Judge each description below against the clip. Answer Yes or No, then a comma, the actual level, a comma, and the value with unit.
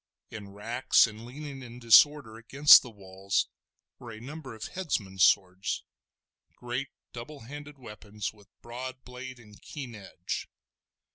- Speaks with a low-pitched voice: Yes, low, 120 Hz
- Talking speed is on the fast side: No, slow, 135 wpm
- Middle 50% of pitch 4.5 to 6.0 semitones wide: No, average, 4.0 semitones